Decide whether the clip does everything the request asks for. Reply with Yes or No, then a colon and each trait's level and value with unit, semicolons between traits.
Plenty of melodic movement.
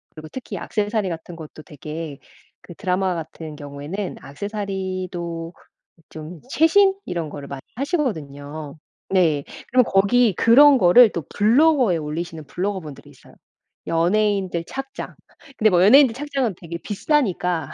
Yes: wide, 5.8 semitones